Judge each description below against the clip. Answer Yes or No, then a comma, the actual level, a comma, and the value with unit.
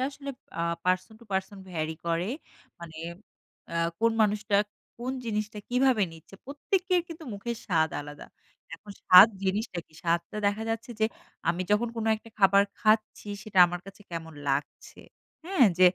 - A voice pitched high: Yes, high, 205 Hz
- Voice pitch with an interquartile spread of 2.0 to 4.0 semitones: No, average, 4.9 semitones